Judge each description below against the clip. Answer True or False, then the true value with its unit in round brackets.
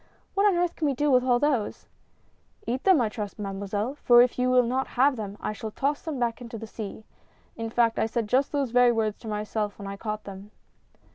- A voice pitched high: True (235 Hz)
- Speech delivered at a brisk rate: True (255 wpm)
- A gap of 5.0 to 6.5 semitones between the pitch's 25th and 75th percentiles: False (3.6 semitones)